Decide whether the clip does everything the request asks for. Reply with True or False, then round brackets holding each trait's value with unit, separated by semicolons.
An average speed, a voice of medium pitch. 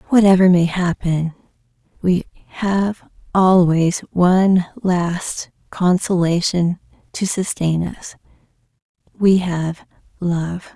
False (80 wpm; 175 Hz)